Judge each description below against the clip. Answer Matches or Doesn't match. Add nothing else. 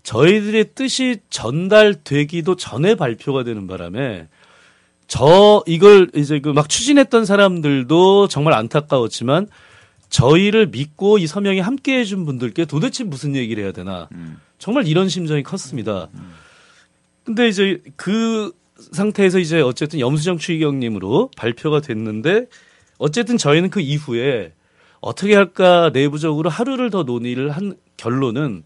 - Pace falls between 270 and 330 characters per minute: Matches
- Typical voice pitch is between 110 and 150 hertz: Doesn't match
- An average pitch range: Doesn't match